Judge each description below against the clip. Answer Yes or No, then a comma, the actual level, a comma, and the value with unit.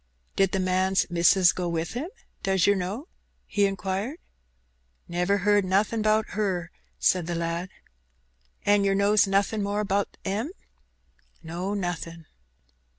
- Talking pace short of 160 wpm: Yes, slow, 135 wpm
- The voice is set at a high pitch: Yes, high, 195 Hz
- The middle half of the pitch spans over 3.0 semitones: No, narrow, 2.5 semitones